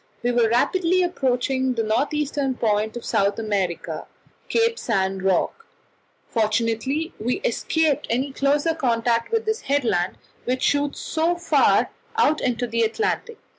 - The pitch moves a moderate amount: No, wide, 5.8 semitones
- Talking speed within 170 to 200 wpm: No, slow, 135 wpm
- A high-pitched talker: Yes, very high, 255 Hz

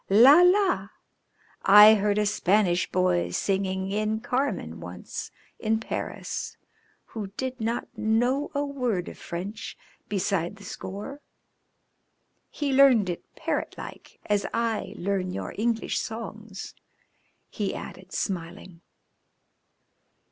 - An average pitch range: Yes, average, 3.7 semitones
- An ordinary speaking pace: No, slow, 110 wpm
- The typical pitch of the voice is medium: No, high, 210 Hz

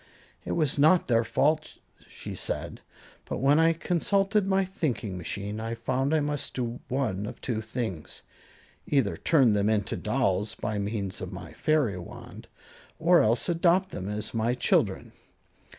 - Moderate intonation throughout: No, wide, 7.0 semitones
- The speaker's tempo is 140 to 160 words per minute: Yes, average, 155 wpm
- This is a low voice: Yes, low, 120 Hz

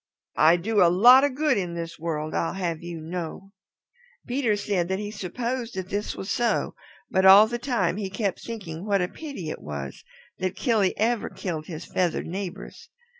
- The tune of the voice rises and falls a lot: No, average, 4.7 semitones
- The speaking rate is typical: Yes, average, 185 wpm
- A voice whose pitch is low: No, high, 190 Hz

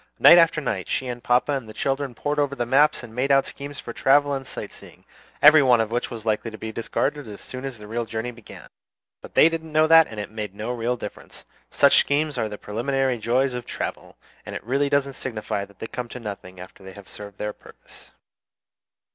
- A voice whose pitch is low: Yes, low, 125 Hz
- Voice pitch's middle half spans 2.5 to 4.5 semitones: Yes, average, 4.2 semitones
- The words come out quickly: Yes, fast, 225 wpm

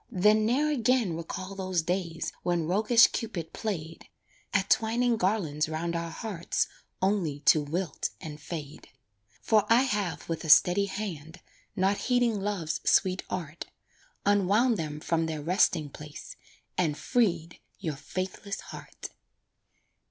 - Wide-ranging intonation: No, average, 4.5 semitones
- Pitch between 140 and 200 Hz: Yes, medium, 185 Hz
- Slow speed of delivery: Yes, slow, 130 wpm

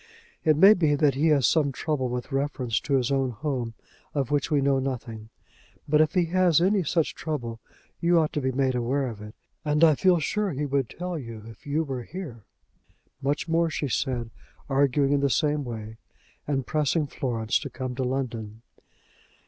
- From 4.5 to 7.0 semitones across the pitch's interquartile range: No, average, 3.7 semitones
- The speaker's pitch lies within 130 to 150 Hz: Yes, medium, 140 Hz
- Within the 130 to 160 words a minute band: No, average, 195 wpm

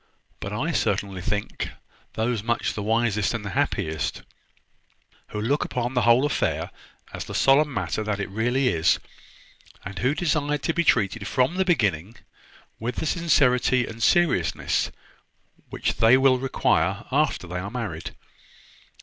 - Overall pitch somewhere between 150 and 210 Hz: No, low, 120 Hz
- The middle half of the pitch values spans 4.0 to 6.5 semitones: Yes, average, 5.1 semitones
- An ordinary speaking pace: Yes, average, 150 wpm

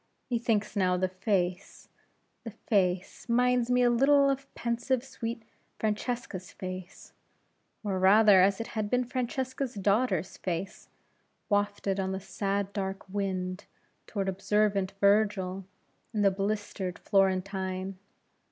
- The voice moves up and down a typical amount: Yes, average, 3.5 semitones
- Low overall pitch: No, high, 200 Hz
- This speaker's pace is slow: Yes, slow, 120 wpm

